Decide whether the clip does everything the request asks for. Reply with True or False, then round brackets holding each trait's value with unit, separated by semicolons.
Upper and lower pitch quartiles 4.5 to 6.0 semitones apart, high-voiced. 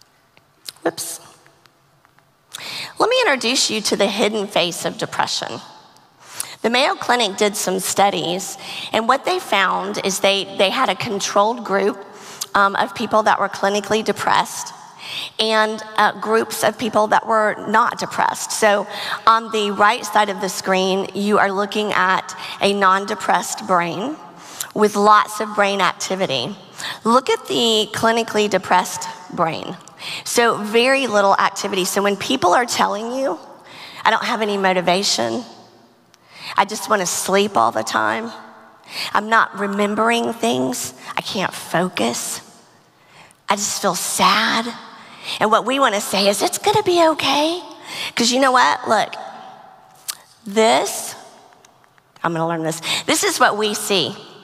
False (2.6 semitones; 205 Hz)